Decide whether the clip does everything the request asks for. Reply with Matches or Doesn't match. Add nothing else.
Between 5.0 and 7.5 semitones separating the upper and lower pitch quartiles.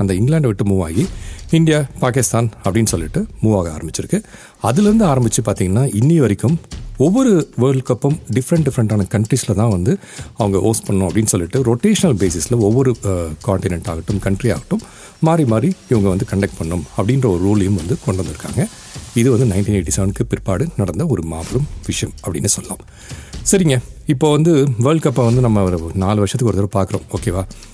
Matches